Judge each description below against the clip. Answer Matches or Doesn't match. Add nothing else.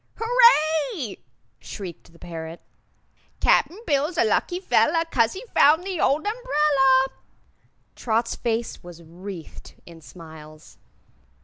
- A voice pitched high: Matches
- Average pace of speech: Doesn't match